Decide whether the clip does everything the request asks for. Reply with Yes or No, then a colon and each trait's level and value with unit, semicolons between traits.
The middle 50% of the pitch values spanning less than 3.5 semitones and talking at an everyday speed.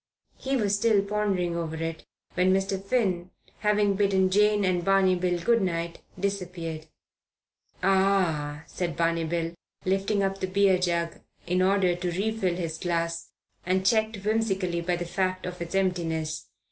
Yes: narrow, 2.5 semitones; average, 150 wpm